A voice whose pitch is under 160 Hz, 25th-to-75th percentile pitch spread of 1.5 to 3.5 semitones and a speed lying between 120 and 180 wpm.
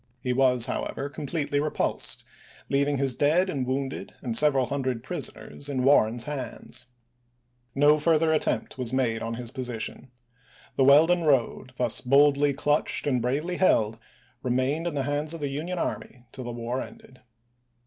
Yes: low, 135 Hz; average, 2.8 semitones; average, 155 wpm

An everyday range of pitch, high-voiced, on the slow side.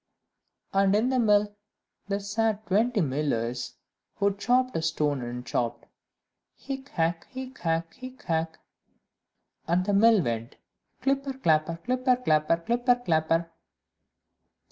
No: wide, 7.4 semitones; high, 200 Hz; slow, 120 wpm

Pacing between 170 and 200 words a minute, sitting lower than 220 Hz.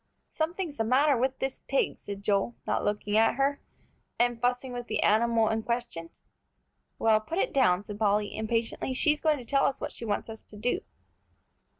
No: average, 190 wpm; high, 235 Hz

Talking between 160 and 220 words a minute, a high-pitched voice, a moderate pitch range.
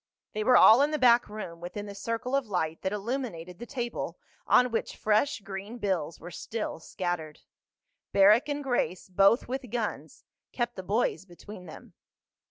Yes: average, 170 wpm; high, 210 Hz; average, 4.8 semitones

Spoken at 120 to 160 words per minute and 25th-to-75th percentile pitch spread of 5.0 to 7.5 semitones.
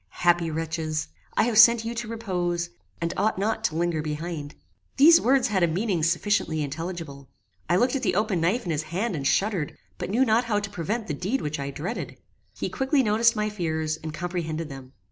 No: average, 200 wpm; wide, 5.6 semitones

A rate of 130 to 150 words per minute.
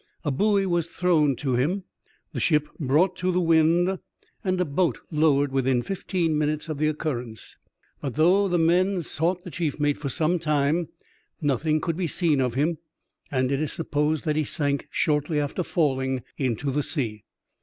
No: average, 175 wpm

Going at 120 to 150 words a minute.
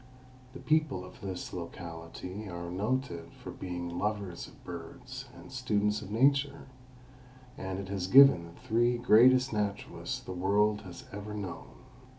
Yes: average, 145 wpm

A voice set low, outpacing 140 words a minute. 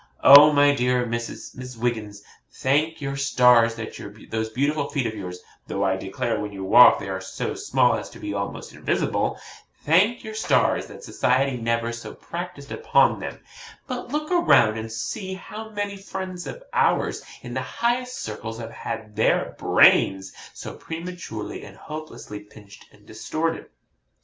Yes: low, 125 Hz; average, 160 wpm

